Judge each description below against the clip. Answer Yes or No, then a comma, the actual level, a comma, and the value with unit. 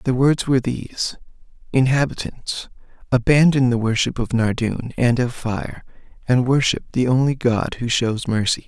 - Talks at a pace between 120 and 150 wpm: Yes, average, 145 wpm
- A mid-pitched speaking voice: No, low, 125 Hz